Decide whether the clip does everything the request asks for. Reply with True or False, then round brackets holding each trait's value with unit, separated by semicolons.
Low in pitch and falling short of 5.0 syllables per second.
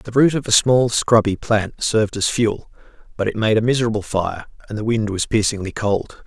False (110 Hz; 5.2 syllables/s)